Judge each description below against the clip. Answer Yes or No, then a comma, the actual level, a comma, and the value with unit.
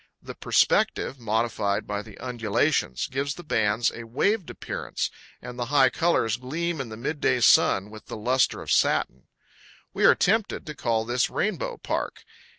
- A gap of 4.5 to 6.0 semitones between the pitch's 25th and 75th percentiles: Yes, average, 5.0 semitones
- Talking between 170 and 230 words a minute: No, average, 160 wpm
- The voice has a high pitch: No, low, 125 Hz